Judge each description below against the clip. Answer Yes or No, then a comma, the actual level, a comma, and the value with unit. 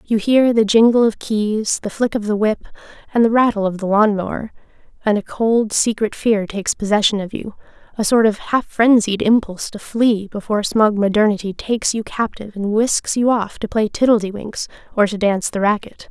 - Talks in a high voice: Yes, high, 215 Hz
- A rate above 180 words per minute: Yes, average, 190 wpm